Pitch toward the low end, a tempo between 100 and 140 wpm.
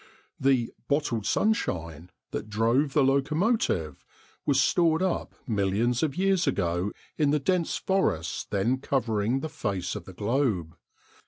Yes: low, 130 Hz; slow, 135 wpm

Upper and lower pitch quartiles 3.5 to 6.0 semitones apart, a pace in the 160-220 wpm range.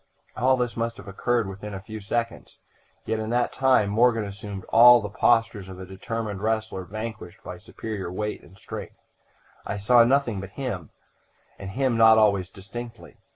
No: average, 3.1 semitones; average, 170 wpm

